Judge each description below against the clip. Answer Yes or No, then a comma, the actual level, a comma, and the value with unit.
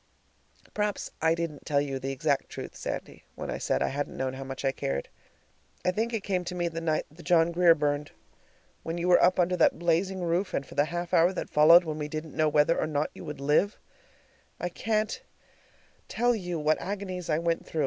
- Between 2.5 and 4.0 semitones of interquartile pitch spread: Yes, average, 3.3 semitones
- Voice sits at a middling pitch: Yes, medium, 165 Hz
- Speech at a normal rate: No, fast, 220 wpm